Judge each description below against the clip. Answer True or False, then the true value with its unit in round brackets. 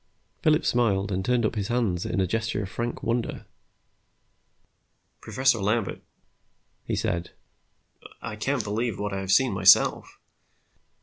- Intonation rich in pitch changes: False (3.7 semitones)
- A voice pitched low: True (105 Hz)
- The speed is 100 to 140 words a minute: True (135 wpm)